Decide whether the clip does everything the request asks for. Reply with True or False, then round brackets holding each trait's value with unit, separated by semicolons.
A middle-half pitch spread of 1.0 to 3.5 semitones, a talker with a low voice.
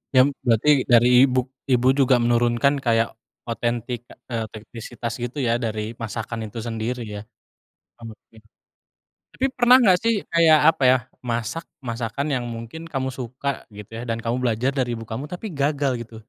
True (3.0 semitones; 120 Hz)